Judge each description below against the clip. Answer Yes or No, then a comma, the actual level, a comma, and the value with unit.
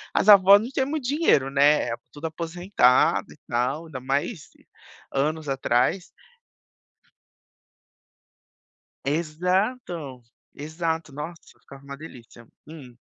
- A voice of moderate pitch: Yes, medium, 155 Hz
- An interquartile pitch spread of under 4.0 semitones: No, average, 4.8 semitones